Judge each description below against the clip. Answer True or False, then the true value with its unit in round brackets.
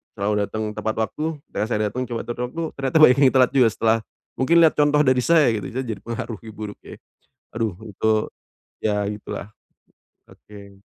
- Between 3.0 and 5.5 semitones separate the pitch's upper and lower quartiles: True (3.6 semitones)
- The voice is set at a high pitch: False (115 Hz)